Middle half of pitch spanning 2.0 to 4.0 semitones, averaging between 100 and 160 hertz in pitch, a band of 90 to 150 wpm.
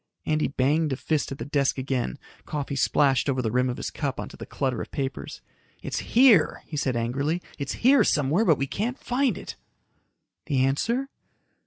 No: average, 3.6 semitones; medium, 140 Hz; average, 185 wpm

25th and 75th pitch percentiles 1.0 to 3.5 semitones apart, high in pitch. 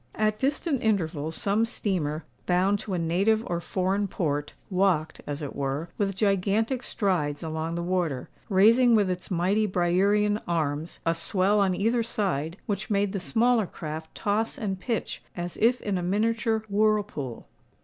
No: average, 4.1 semitones; high, 195 Hz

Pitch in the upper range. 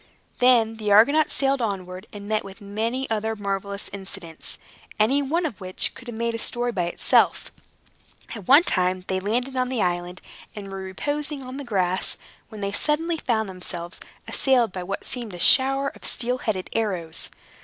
Yes: high, 215 Hz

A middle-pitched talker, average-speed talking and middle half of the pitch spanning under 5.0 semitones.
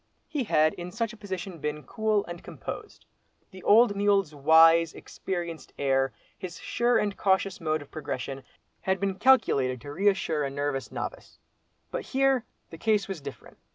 No: medium, 175 Hz; average, 160 wpm; average, 5.3 semitones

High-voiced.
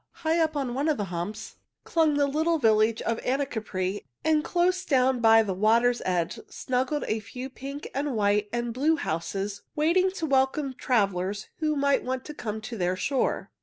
Yes: very high, 250 Hz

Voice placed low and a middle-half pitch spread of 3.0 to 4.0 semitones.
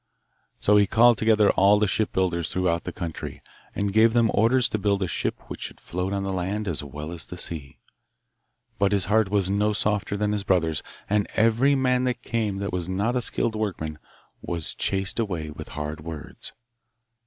Yes: low, 100 Hz; average, 3.6 semitones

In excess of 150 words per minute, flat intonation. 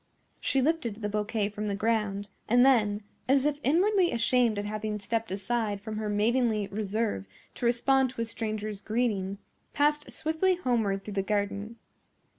No: average, 160 wpm; average, 3.3 semitones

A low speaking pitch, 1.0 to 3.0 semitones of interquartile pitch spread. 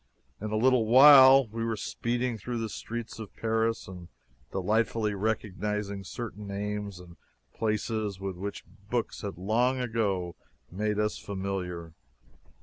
Yes: low, 105 Hz; average, 2.7 semitones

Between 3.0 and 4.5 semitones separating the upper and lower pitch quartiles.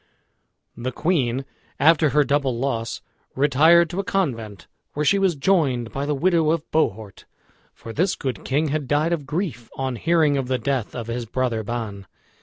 No: average, 4.9 semitones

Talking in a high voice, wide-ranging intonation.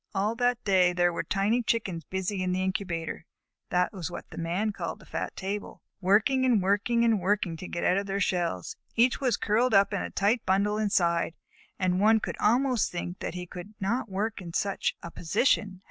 No: high, 195 Hz; average, 3.3 semitones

